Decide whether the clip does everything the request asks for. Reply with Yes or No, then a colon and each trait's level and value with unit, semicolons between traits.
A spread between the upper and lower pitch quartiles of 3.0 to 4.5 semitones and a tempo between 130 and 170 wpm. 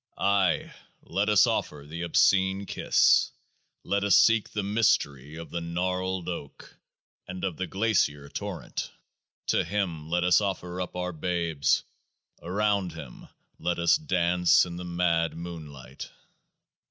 No: narrow, 2.5 semitones; slow, 135 wpm